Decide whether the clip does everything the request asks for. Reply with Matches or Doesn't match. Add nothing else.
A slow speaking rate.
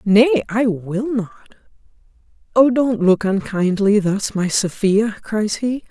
Matches